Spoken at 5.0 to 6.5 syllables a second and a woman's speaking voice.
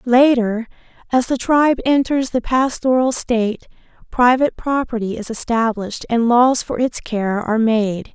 No: 4.7 syllables/s; female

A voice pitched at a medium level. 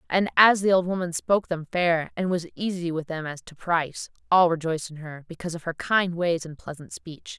Yes: medium, 170 Hz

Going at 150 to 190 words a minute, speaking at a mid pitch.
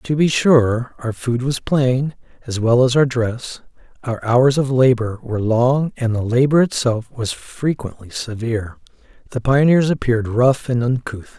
No: average, 165 wpm; low, 125 Hz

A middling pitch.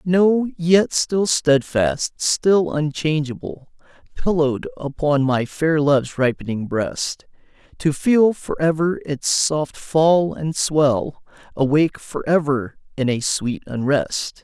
Yes: medium, 150 Hz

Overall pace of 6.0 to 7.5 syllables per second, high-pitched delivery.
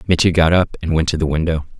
No: 6.7 syllables/s; very low, 80 Hz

